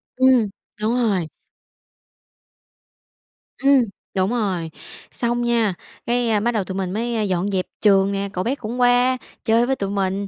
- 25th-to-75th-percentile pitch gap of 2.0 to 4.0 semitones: Yes, average, 3.7 semitones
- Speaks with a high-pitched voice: Yes, high, 220 Hz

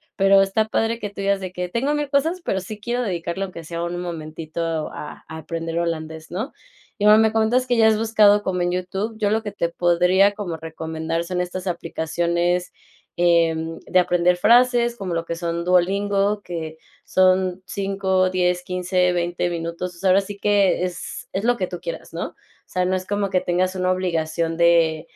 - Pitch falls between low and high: Yes, medium, 180 Hz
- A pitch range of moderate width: Yes, average, 3.1 semitones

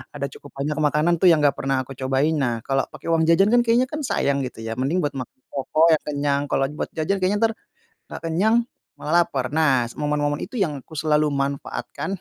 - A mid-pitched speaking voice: Yes, medium, 150 Hz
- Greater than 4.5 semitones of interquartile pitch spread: No, average, 3.4 semitones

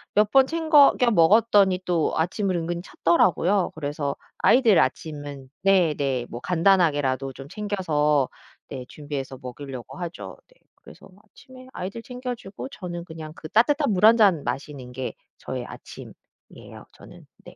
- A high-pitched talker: No, medium, 175 Hz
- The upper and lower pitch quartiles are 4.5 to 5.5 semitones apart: No, wide, 6.4 semitones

